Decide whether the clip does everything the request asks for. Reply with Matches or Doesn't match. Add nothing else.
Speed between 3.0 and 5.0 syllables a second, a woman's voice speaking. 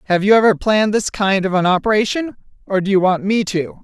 Doesn't match